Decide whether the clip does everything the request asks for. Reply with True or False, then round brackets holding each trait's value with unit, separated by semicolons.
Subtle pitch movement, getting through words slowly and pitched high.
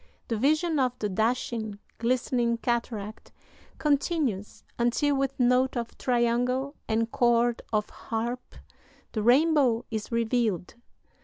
True (2.3 semitones; 110 wpm; 240 Hz)